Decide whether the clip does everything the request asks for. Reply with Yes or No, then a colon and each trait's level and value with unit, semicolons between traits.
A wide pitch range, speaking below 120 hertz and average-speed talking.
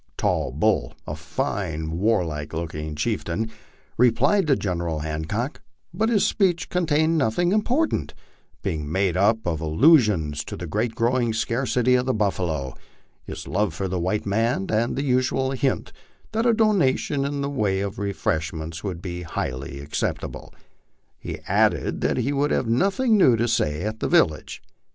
Yes: wide, 8.5 semitones; low, 110 Hz; average, 155 wpm